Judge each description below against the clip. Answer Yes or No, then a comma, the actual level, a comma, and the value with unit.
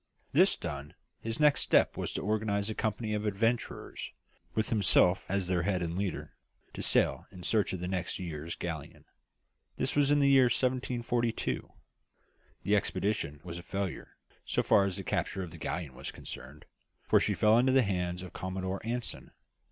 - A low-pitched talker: Yes, low, 100 Hz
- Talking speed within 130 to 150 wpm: No, average, 175 wpm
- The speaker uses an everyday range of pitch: Yes, average, 4.2 semitones